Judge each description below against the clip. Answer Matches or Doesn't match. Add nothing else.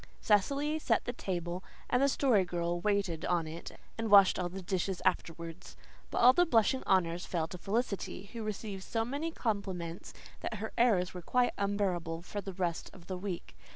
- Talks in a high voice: Matches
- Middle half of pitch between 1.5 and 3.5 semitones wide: Doesn't match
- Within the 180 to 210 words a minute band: Matches